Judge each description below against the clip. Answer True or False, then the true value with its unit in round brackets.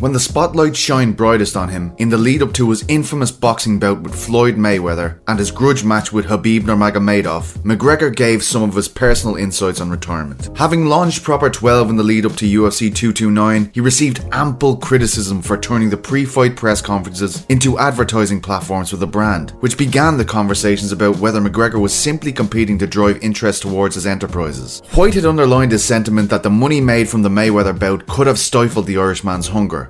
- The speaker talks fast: False (190 wpm)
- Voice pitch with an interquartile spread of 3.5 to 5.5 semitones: True (3.9 semitones)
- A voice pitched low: True (110 Hz)